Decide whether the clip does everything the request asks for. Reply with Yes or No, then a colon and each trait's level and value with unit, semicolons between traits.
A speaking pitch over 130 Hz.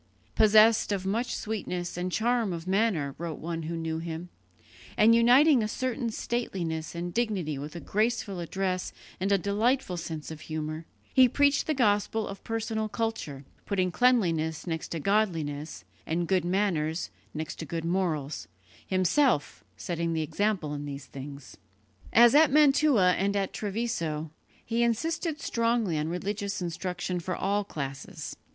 Yes: medium, 185 Hz